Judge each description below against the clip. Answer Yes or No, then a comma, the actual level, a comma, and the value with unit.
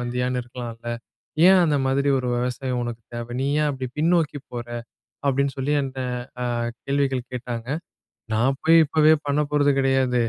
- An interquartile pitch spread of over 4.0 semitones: No, narrow, 2.6 semitones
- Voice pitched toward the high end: No, low, 130 Hz